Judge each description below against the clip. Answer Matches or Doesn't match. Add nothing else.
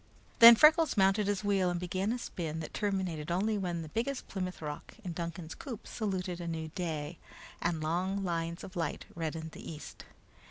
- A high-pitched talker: Doesn't match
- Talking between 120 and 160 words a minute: Doesn't match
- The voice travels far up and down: Doesn't match